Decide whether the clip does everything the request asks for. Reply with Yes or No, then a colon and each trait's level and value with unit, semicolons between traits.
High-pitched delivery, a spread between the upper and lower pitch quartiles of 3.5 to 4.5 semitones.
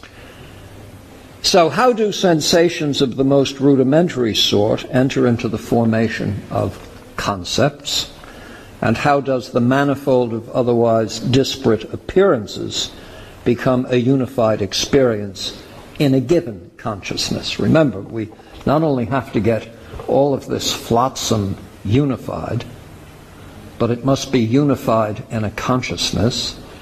No: low, 120 Hz; average, 4.2 semitones